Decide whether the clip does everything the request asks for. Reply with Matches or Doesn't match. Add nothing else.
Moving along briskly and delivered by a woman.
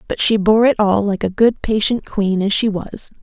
Matches